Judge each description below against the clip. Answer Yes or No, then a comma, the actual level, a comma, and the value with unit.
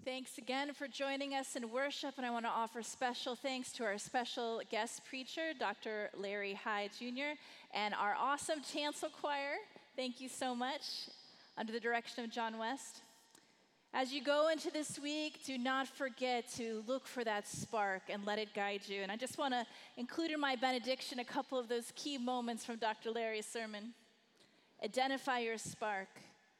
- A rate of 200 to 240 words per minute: No, average, 180 wpm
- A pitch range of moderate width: Yes, average, 3.5 semitones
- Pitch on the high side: Yes, very high, 250 Hz